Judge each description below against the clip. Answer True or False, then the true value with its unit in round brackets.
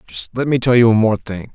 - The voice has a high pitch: False (110 Hz)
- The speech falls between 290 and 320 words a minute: True (310 wpm)